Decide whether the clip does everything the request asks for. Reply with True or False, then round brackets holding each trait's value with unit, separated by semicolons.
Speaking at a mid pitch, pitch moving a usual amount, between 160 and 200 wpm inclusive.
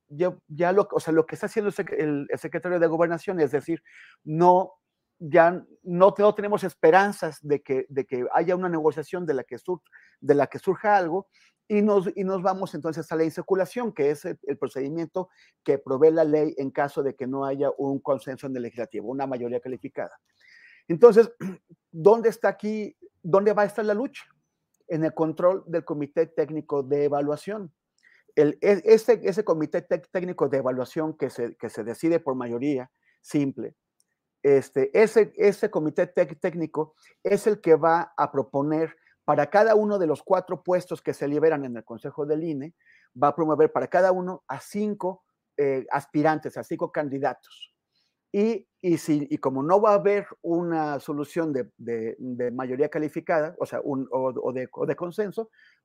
True (165 Hz; 4.9 semitones; 180 wpm)